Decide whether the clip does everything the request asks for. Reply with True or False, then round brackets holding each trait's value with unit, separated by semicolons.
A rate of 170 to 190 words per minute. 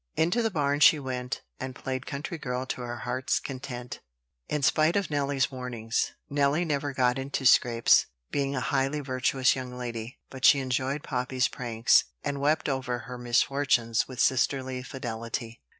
False (160 wpm)